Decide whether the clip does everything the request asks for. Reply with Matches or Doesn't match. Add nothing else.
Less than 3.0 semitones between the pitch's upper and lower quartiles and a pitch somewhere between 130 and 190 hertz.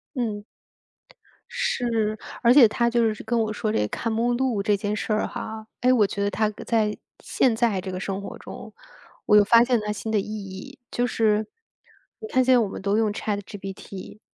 Doesn't match